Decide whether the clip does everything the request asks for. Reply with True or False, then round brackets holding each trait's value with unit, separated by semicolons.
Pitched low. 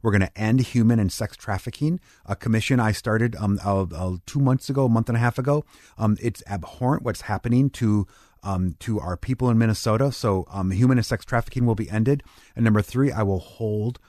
True (115 Hz)